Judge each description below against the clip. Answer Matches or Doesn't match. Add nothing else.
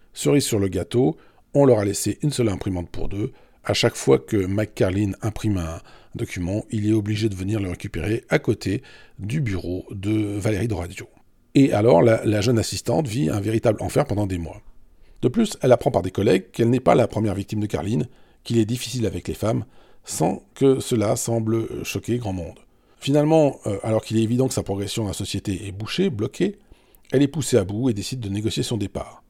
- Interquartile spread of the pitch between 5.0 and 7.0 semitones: Doesn't match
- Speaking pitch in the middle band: Doesn't match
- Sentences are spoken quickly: Doesn't match